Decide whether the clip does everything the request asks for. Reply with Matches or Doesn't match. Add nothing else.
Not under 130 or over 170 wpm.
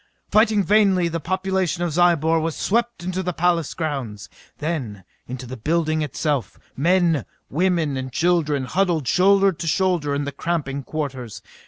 Matches